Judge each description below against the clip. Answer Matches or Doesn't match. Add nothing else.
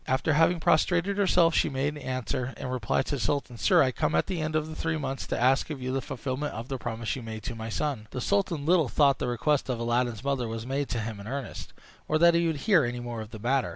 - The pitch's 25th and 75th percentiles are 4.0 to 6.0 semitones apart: Matches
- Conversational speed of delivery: Doesn't match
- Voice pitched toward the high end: Doesn't match